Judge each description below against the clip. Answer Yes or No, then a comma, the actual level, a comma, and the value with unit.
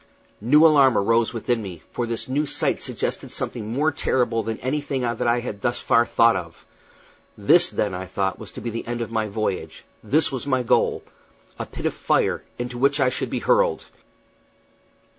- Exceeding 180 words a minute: Yes, average, 190 wpm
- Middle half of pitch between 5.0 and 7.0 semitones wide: No, average, 3.6 semitones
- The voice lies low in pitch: Yes, low, 120 Hz